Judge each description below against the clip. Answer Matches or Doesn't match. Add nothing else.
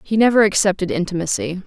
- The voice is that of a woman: Matches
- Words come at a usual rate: Matches